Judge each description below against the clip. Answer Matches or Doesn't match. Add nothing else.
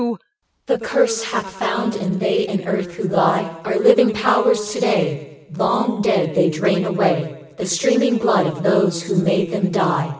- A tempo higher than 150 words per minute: Matches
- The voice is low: Doesn't match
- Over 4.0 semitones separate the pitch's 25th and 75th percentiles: Doesn't match